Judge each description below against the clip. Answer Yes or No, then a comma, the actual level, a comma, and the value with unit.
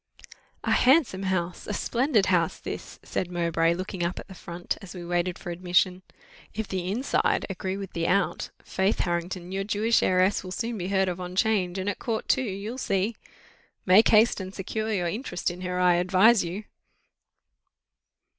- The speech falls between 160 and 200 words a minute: Yes, average, 180 wpm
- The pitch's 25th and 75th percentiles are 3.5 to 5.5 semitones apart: No, average, 2.7 semitones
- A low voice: No, medium, 185 Hz